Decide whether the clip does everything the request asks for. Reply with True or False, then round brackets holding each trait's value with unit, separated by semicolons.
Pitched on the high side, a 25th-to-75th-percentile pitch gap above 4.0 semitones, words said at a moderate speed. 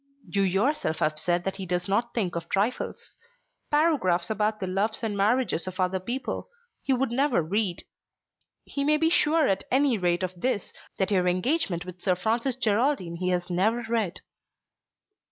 True (200 Hz; 5.4 semitones; 170 wpm)